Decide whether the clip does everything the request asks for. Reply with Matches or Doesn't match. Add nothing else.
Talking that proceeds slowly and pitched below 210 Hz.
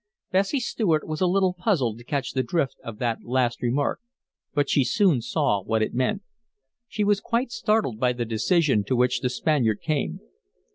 Doesn't match